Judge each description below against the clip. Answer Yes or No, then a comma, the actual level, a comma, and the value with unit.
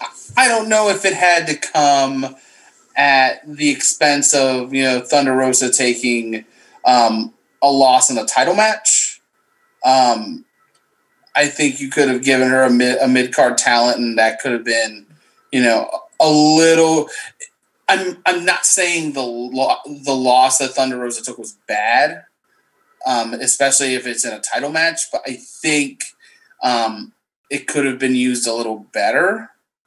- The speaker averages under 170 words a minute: Yes, average, 160 wpm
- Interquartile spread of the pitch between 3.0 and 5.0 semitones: No, wide, 5.6 semitones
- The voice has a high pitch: No, low, 135 Hz